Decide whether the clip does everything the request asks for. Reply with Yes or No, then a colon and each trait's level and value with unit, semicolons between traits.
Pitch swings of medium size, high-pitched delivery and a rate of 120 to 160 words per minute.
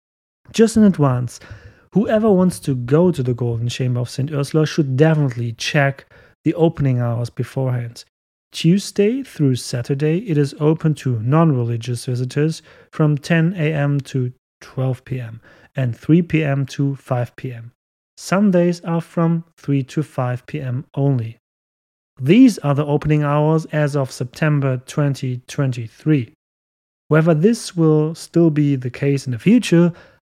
No: average, 4.2 semitones; medium, 140 Hz; average, 140 wpm